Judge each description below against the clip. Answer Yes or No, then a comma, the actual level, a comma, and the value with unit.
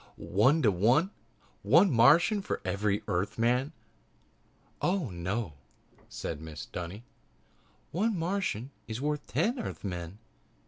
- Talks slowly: Yes, slow, 105 wpm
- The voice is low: Yes, low, 120 Hz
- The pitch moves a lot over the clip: Yes, wide, 8.8 semitones